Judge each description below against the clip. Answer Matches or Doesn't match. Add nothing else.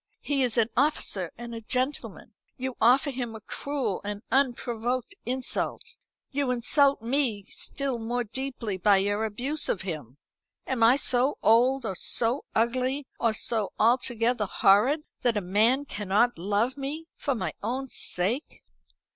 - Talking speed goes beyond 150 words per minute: Doesn't match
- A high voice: Matches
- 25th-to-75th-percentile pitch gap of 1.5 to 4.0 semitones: Matches